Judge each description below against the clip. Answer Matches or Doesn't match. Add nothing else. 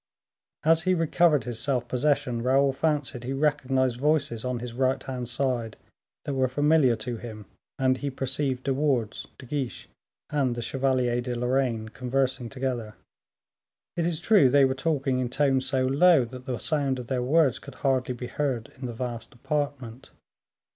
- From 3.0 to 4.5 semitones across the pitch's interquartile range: Doesn't match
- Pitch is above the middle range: Doesn't match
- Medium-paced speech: Matches